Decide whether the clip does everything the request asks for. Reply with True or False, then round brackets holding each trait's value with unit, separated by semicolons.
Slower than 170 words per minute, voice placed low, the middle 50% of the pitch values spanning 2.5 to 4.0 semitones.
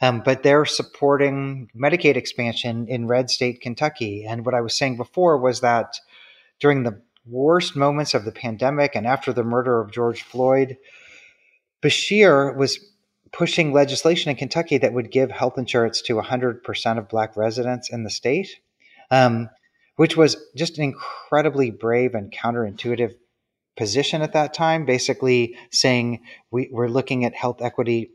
True (155 wpm; 125 Hz; 3.1 semitones)